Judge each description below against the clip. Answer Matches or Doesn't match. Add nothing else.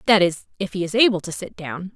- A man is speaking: Doesn't match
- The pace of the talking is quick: Matches